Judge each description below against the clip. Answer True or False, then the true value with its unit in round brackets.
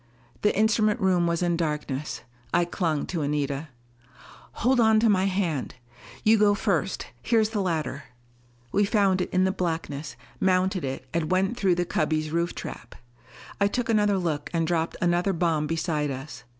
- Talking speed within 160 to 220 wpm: True (170 wpm)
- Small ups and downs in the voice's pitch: False (4.3 semitones)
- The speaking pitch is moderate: True (175 Hz)